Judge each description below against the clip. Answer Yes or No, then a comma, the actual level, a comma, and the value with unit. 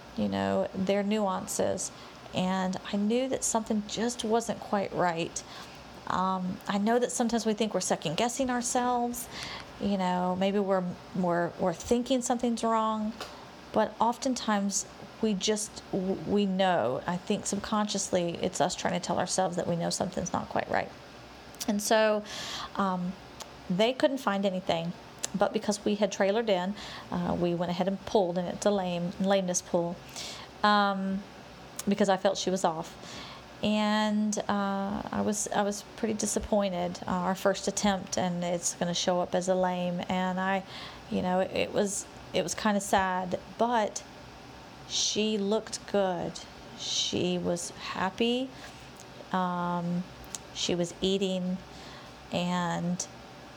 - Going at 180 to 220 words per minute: No, average, 150 wpm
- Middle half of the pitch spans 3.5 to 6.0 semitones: No, average, 2.7 semitones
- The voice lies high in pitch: Yes, high, 195 Hz